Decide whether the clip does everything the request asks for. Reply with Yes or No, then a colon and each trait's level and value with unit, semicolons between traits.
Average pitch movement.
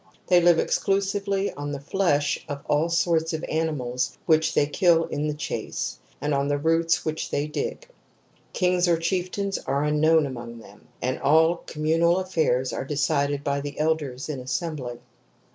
Yes: average, 3.0 semitones